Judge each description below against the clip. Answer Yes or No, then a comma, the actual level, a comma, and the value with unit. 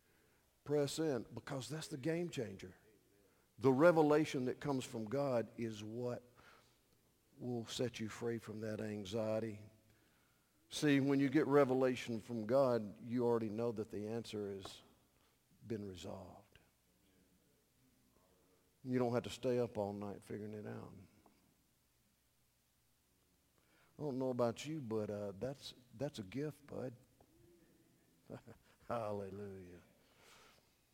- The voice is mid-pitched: No, low, 115 Hz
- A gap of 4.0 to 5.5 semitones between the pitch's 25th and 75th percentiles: Yes, average, 4.3 semitones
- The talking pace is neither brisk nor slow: No, slow, 120 wpm